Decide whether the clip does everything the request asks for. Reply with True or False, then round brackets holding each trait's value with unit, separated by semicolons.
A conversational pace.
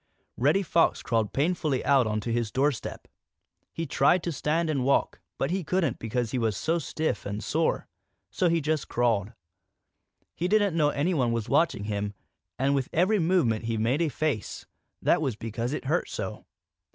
True (175 wpm)